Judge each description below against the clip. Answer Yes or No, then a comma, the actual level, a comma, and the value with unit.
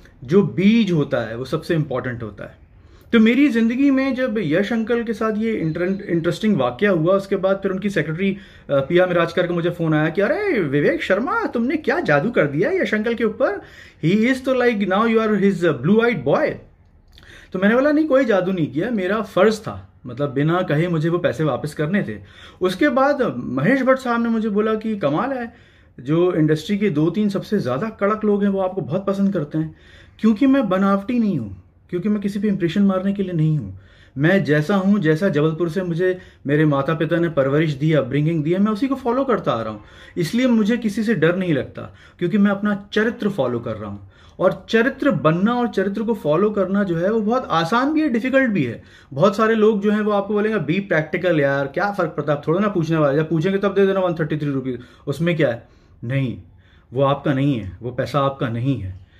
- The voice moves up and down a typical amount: No, wide, 6.8 semitones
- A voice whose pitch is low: No, medium, 180 Hz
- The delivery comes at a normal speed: No, fast, 220 wpm